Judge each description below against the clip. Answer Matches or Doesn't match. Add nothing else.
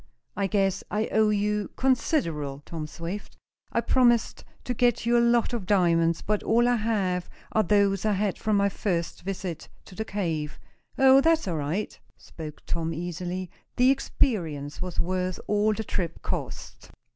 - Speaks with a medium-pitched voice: Doesn't match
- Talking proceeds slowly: Doesn't match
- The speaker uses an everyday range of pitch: Matches